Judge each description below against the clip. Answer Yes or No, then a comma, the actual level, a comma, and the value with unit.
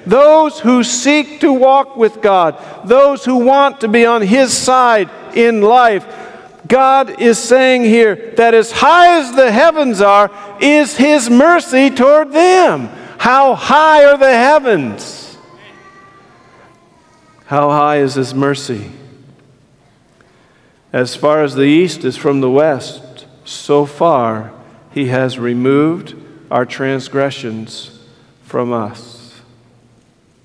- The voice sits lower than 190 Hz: No, high, 205 Hz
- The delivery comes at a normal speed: No, slow, 120 wpm